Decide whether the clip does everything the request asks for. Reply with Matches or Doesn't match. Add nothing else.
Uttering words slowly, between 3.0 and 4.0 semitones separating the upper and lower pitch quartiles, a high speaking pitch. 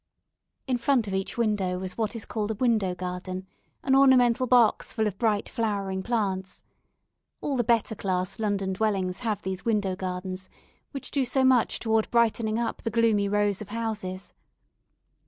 Doesn't match